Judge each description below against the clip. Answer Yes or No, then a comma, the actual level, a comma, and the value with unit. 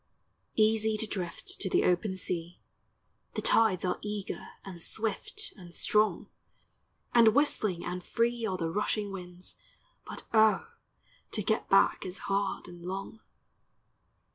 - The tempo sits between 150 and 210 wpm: No, slow, 135 wpm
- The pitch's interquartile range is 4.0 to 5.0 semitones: No, average, 3.2 semitones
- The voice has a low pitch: No, high, 200 Hz